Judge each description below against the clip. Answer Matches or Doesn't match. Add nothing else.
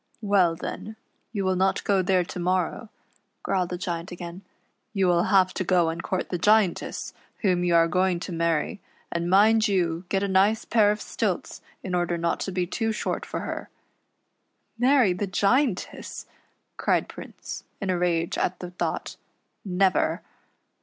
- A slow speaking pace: Doesn't match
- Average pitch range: Doesn't match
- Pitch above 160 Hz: Matches